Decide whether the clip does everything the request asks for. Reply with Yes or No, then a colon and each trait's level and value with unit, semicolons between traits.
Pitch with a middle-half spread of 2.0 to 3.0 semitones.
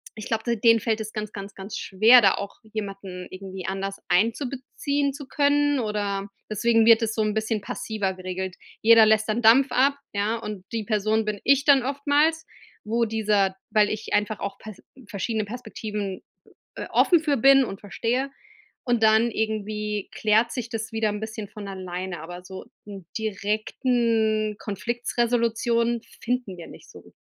Yes: average, 2.7 semitones